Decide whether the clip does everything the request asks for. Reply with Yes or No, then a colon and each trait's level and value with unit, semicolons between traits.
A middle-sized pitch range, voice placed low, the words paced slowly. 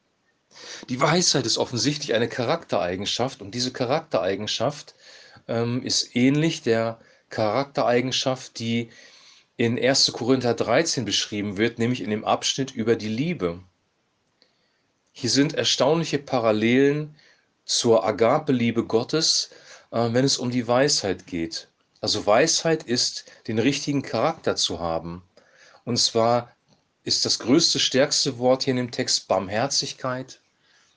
Yes: average, 3.4 semitones; low, 125 Hz; slow, 120 wpm